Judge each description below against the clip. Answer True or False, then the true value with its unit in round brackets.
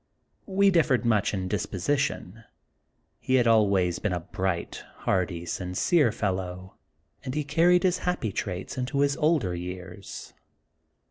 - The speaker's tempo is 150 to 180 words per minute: False (135 wpm)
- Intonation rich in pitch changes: True (7.7 semitones)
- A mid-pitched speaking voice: False (105 Hz)